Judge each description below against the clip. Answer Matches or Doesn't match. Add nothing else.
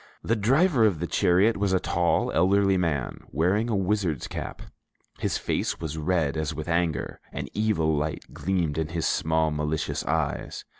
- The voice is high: Doesn't match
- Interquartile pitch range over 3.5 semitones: Matches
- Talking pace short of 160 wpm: Doesn't match